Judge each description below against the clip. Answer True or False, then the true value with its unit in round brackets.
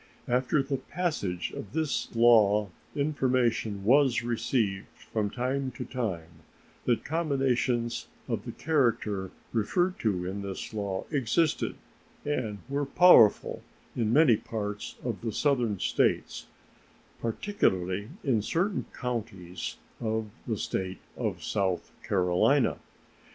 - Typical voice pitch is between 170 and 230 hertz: False (115 Hz)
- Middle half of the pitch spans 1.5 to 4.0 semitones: False (5.1 semitones)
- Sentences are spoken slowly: True (115 wpm)